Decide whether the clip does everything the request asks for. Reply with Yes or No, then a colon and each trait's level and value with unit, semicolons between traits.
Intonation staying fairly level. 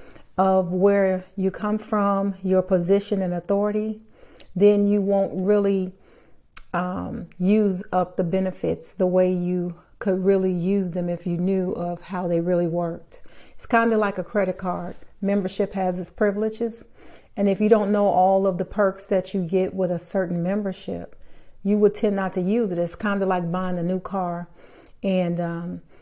Yes: narrow, 1.8 semitones